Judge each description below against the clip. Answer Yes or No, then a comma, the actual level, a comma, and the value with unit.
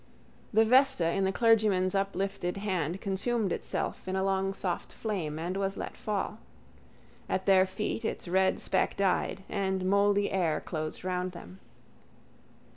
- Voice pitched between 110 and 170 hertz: No, high, 190 Hz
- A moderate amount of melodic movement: No, narrow, 1.6 semitones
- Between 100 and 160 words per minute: Yes, average, 145 wpm